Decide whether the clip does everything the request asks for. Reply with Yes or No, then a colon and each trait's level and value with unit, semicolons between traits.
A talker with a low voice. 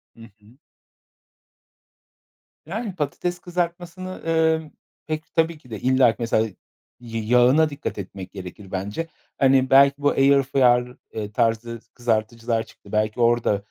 Yes: low, 125 Hz